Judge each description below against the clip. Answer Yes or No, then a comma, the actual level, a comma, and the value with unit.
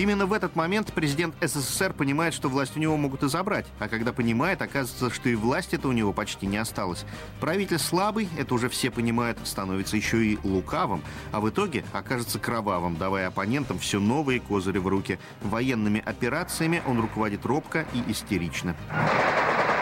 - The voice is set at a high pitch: No, low, 120 Hz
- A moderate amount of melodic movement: No, wide, 6.4 semitones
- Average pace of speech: No, fast, 170 wpm